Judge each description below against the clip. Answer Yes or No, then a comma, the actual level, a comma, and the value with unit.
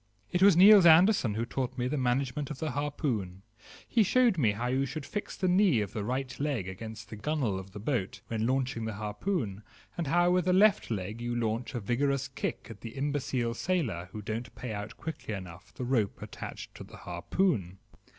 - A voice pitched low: Yes, low, 125 Hz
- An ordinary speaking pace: No, fast, 210 wpm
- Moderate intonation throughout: No, wide, 6.1 semitones